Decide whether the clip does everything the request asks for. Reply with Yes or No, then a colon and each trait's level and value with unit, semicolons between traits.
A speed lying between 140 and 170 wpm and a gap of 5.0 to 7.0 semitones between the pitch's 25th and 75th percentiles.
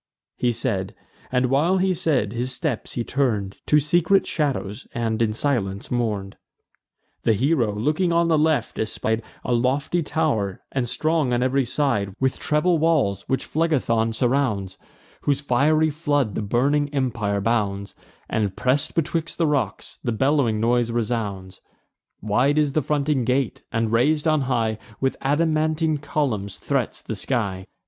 Yes: average, 150 wpm; average, 5.3 semitones